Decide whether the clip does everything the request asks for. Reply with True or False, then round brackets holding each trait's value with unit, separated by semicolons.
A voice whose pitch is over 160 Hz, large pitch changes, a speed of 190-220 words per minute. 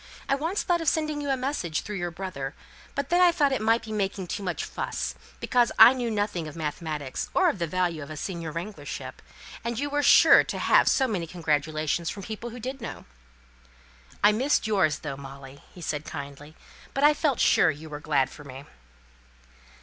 True (190 Hz; 8.9 semitones; 205 wpm)